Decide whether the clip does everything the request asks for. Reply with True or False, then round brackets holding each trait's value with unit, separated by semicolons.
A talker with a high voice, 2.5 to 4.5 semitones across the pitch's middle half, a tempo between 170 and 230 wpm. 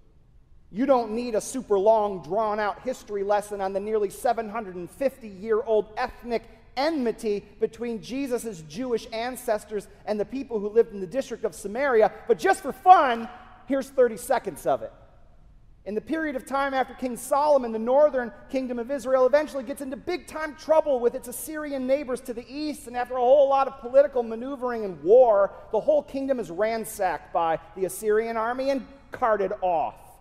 True (240 Hz; 4.2 semitones; 175 wpm)